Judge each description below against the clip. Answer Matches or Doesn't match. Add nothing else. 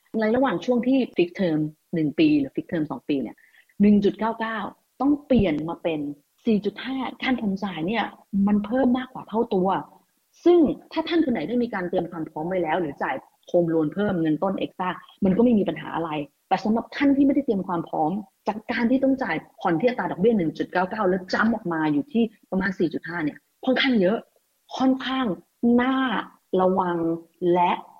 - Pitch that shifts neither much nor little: Doesn't match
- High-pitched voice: Matches